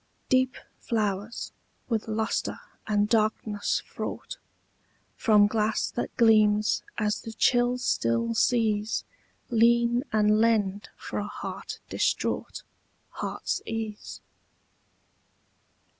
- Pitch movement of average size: No, narrow, 1.8 semitones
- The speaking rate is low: Yes, slow, 95 wpm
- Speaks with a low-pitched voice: No, high, 220 Hz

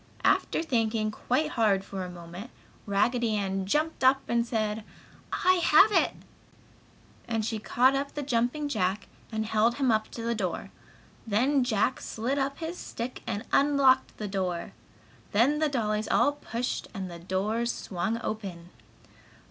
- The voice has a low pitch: No, high, 230 Hz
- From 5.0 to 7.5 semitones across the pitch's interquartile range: No, average, 4.5 semitones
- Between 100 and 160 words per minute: Yes, average, 155 wpm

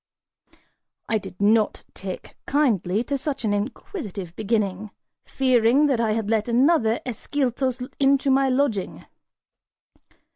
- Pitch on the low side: No, high, 235 Hz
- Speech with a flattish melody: No, average, 4.4 semitones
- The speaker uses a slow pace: Yes, slow, 115 wpm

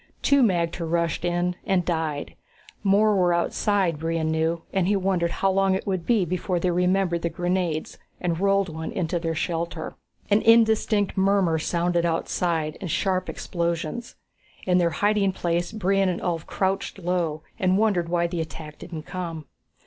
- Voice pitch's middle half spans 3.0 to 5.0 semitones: No, narrow, 2.6 semitones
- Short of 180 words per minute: Yes, average, 165 wpm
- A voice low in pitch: No, medium, 175 Hz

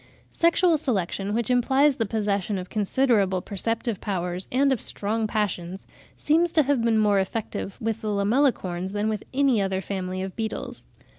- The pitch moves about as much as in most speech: Yes, average, 4.5 semitones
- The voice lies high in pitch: Yes, high, 215 Hz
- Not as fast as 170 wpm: Yes, average, 160 wpm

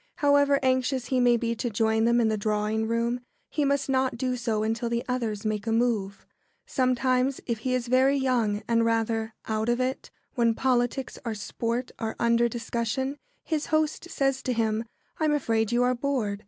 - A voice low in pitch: No, high, 240 Hz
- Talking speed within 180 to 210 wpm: Yes, average, 185 wpm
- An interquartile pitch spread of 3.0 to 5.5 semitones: No, narrow, 2.6 semitones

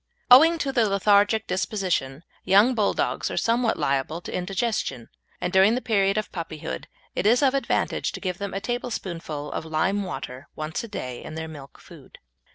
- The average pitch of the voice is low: No, high, 195 Hz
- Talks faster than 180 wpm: No, average, 175 wpm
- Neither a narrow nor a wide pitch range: No, wide, 5.8 semitones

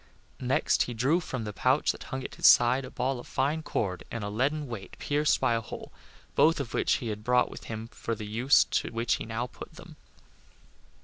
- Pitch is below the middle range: Yes, low, 125 Hz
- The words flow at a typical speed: No, fast, 225 wpm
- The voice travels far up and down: No, average, 3.7 semitones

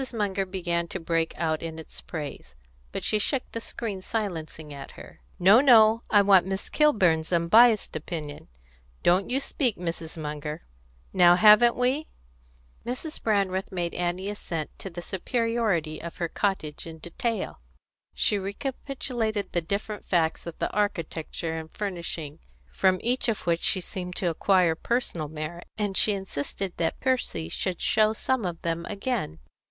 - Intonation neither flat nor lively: Yes, average, 4.6 semitones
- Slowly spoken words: No, average, 155 wpm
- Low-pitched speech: No, medium, 185 Hz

